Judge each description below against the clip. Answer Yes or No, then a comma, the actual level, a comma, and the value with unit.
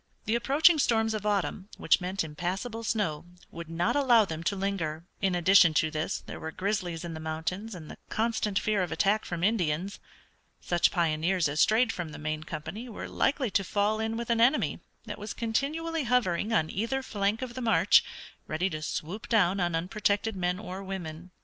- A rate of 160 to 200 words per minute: Yes, average, 190 wpm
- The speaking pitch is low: No, high, 195 Hz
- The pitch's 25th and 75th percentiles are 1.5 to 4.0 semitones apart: No, average, 4.8 semitones